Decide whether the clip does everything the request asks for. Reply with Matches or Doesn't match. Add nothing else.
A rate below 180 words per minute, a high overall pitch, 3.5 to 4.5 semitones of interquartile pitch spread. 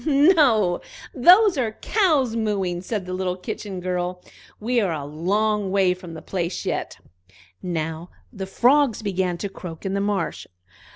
Matches